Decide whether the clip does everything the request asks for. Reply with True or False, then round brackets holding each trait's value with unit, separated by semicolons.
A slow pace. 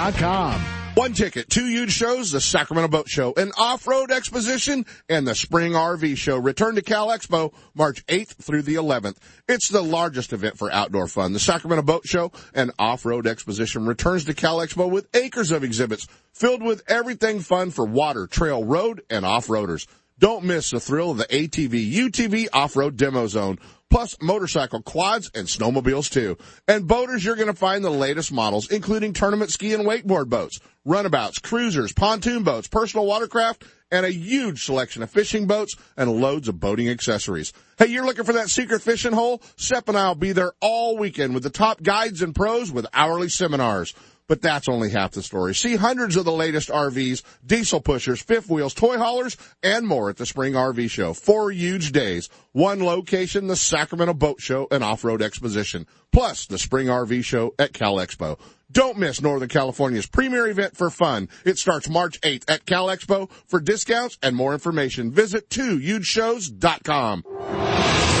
False (175 wpm)